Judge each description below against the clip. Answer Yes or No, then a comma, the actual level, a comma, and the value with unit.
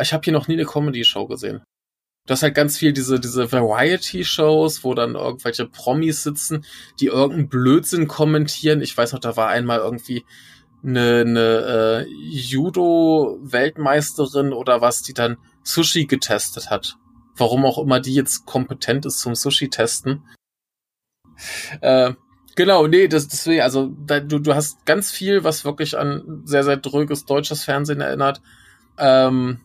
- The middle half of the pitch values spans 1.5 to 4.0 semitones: Yes, average, 3.6 semitones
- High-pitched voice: No, medium, 140 Hz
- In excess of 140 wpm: Yes, average, 150 wpm